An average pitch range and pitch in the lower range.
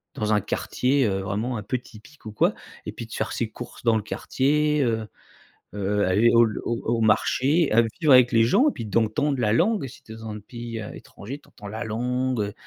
Yes: average, 3.4 semitones; low, 115 Hz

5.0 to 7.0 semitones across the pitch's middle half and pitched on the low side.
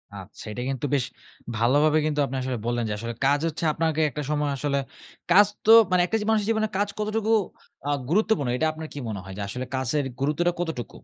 No: wide, 5.5 semitones; medium, 150 Hz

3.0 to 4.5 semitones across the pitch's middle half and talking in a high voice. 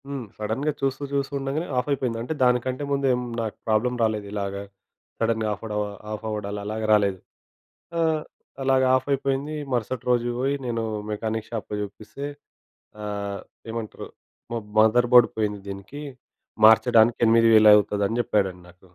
No: average, 3.7 semitones; low, 115 Hz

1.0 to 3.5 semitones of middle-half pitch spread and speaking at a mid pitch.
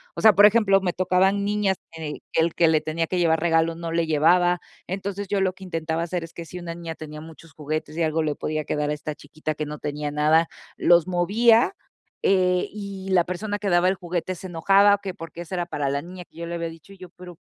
Yes: average, 2.8 semitones; medium, 170 Hz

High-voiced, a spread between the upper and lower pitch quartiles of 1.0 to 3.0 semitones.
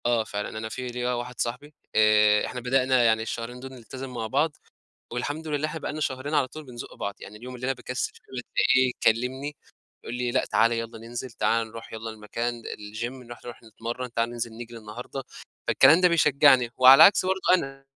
No: low, 125 Hz; narrow, 2.5 semitones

